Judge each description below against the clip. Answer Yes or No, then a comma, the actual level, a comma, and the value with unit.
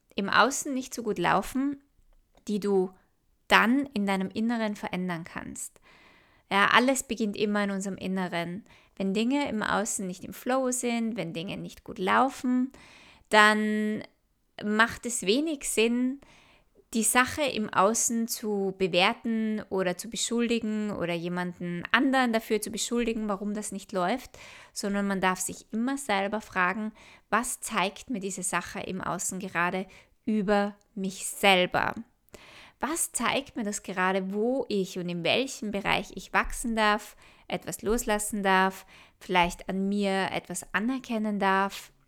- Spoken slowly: No, average, 140 wpm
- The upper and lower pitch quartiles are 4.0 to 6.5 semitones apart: No, average, 3.5 semitones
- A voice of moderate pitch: No, high, 210 Hz